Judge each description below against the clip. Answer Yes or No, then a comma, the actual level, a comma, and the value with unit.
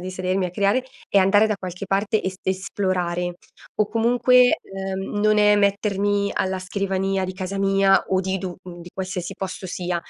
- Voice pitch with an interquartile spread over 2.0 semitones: No, narrow, 1.5 semitones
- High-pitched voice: Yes, high, 195 Hz